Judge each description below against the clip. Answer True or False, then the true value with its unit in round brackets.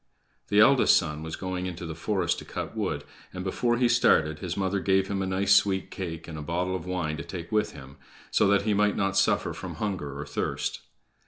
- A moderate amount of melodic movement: True (3.2 semitones)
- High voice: False (95 Hz)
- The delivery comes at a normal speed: False (225 wpm)